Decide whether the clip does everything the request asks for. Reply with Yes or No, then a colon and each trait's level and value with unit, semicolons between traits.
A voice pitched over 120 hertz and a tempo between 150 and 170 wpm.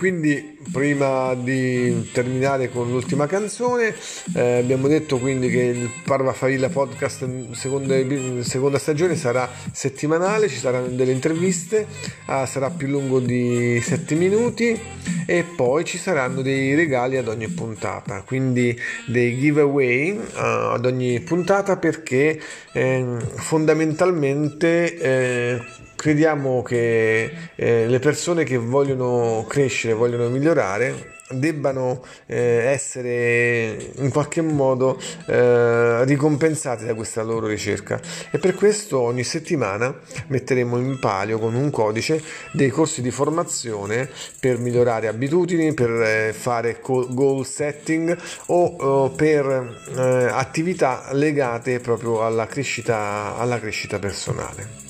No: low, 130 Hz; slow, 115 wpm